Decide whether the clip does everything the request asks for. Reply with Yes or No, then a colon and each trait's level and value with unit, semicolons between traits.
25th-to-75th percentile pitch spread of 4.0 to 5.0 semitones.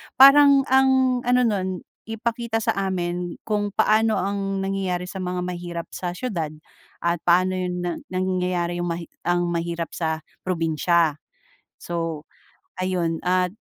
No: average, 3.1 semitones